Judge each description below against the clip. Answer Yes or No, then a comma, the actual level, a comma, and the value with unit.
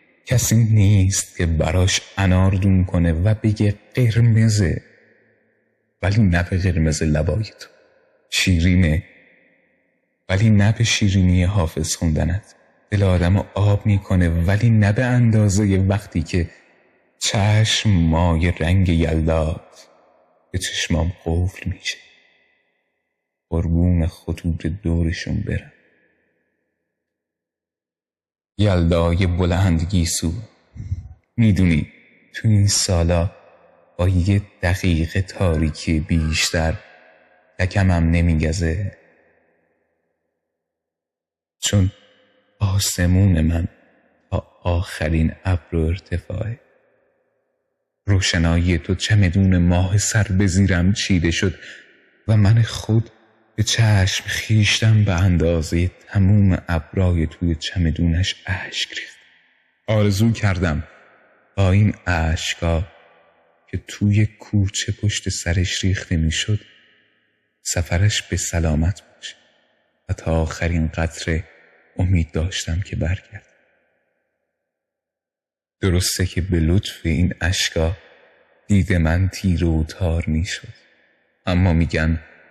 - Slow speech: Yes, slow, 90 wpm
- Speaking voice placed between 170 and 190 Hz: No, very low, 90 Hz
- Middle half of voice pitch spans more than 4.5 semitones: No, average, 3.5 semitones